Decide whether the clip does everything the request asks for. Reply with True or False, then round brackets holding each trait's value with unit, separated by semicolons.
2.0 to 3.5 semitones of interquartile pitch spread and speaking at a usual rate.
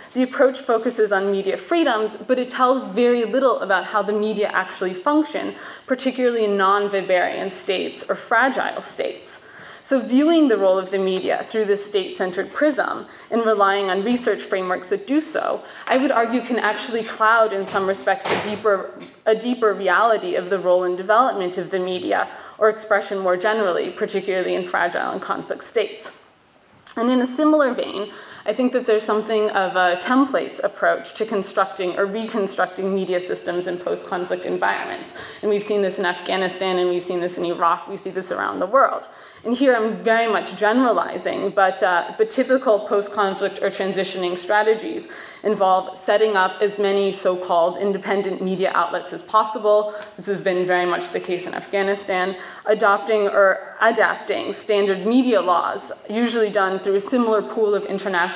True (2.8 semitones; 170 wpm)